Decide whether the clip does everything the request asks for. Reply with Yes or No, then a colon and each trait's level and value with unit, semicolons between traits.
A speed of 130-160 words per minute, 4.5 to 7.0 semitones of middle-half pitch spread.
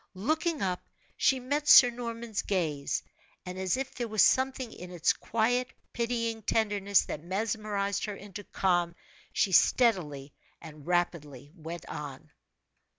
Yes: slow, 135 wpm; average, 5.1 semitones